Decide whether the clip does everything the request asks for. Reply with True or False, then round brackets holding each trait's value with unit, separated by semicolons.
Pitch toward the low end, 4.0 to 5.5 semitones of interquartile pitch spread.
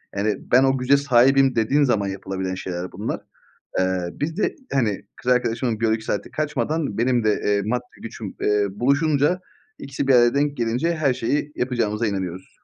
True (120 Hz; 4.8 semitones)